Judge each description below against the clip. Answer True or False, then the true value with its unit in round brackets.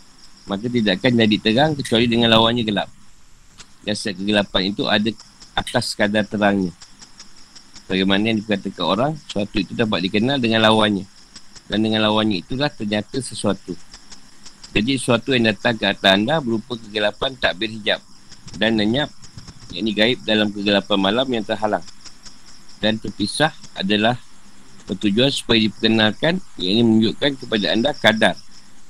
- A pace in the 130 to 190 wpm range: True (135 wpm)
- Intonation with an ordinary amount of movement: False (2.3 semitones)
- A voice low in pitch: True (110 Hz)